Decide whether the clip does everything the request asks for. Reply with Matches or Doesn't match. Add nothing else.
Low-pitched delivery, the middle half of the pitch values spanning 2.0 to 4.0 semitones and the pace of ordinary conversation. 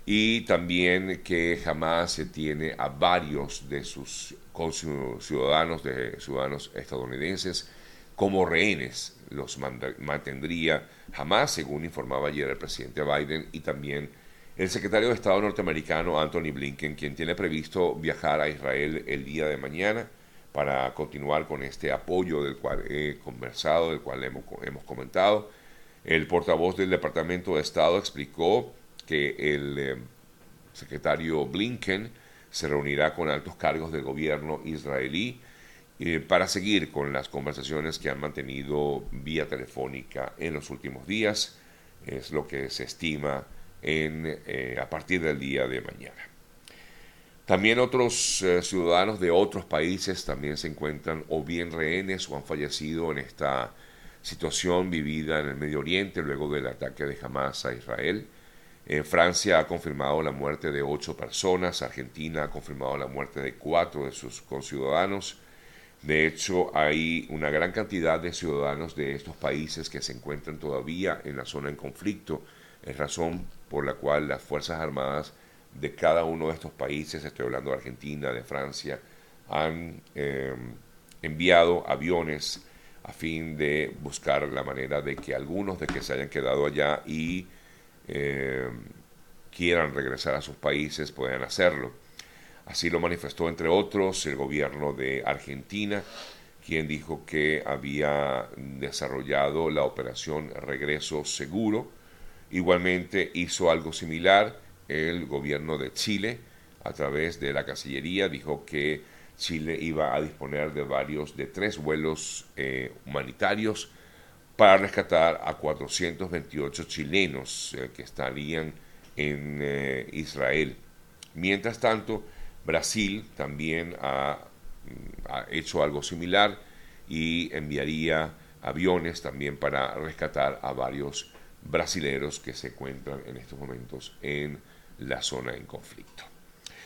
Matches